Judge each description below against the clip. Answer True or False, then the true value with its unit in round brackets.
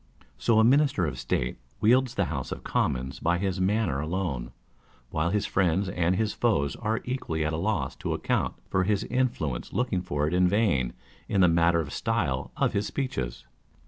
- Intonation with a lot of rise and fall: True (6.0 semitones)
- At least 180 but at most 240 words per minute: True (185 wpm)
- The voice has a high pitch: False (90 Hz)